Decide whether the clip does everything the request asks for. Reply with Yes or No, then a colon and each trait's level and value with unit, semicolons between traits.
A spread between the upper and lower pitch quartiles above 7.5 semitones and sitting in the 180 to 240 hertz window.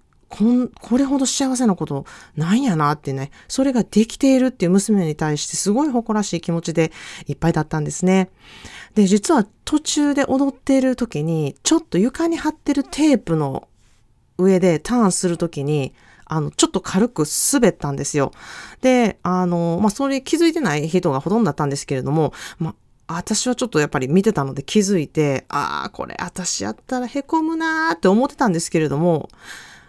Yes: wide, 8.4 semitones; medium, 185 Hz